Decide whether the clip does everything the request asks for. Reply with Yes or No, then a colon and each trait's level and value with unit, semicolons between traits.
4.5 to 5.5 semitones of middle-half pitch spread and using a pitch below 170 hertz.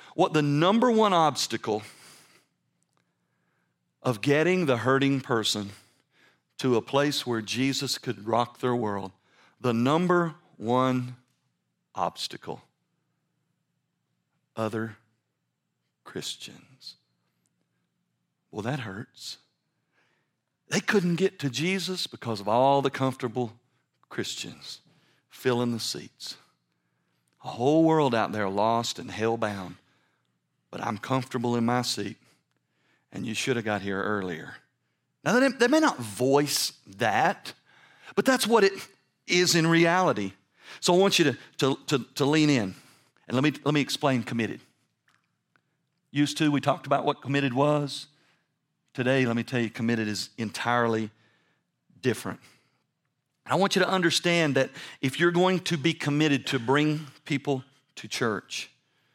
Yes: average, 5.1 semitones; low, 135 Hz